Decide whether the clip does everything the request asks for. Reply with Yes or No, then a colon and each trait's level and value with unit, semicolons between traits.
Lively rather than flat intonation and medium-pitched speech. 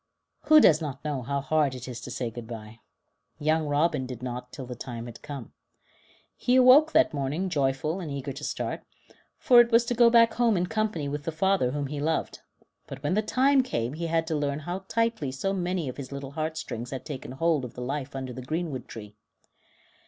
Yes: wide, 5.7 semitones; medium, 150 Hz